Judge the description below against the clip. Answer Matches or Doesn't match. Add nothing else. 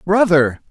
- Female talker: Doesn't match